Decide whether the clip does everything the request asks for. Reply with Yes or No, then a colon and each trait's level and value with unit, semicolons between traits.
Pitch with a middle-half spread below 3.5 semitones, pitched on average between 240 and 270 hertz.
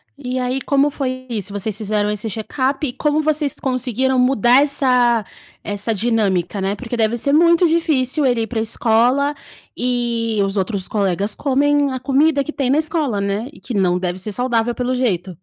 No: average, 4.4 semitones; high, 245 Hz